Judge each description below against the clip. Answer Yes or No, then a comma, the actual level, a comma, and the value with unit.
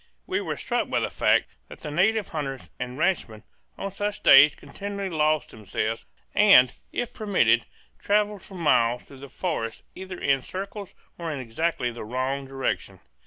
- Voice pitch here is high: No, medium, 155 Hz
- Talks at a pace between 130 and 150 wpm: No, average, 165 wpm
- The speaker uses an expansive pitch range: Yes, wide, 7.4 semitones